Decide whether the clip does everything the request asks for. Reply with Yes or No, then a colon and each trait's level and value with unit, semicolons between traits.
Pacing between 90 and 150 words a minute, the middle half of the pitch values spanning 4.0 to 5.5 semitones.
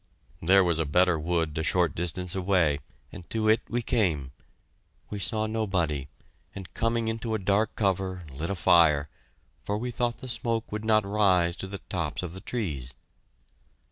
No: average, 170 wpm; average, 4.4 semitones